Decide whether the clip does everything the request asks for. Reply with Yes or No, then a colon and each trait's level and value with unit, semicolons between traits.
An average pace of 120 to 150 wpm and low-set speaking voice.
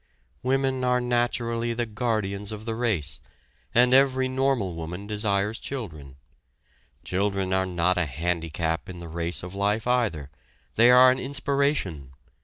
Yes: average, 140 wpm; low, 105 Hz